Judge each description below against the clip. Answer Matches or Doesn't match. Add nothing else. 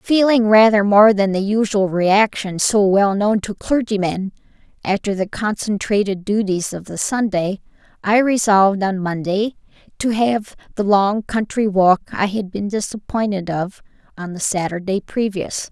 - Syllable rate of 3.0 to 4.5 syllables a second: Matches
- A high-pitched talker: Matches